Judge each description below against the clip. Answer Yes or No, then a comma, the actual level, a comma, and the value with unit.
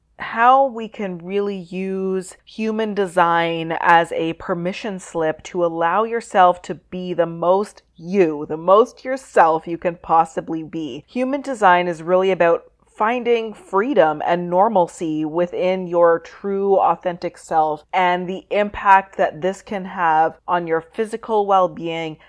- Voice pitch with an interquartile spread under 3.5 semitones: Yes, average, 3.0 semitones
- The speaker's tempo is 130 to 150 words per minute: Yes, average, 140 wpm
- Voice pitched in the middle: Yes, medium, 180 Hz